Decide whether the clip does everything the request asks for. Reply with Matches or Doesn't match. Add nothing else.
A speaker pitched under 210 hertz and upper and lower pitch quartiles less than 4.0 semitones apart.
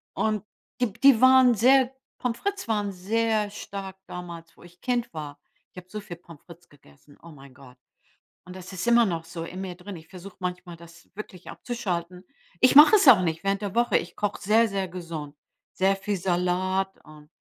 Doesn't match